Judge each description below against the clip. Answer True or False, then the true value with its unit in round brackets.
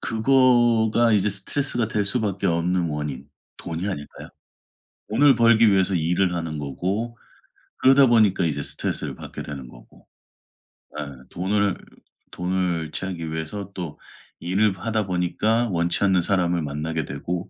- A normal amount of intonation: True (4.7 semitones)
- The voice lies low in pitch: True (95 Hz)